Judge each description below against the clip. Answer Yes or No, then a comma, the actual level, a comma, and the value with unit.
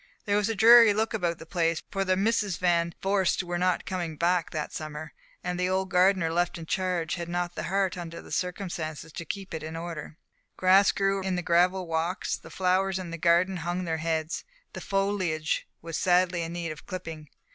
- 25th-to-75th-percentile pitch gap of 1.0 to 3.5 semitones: Yes, narrow, 2.4 semitones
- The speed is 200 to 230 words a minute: Yes, fast, 205 wpm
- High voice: No, medium, 180 Hz